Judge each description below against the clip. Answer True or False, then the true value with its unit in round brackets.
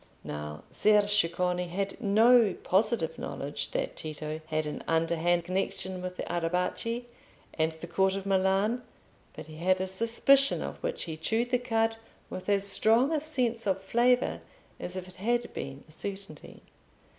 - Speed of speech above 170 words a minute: False (160 wpm)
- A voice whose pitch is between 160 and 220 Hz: True (190 Hz)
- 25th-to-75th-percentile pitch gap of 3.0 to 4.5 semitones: False (5.0 semitones)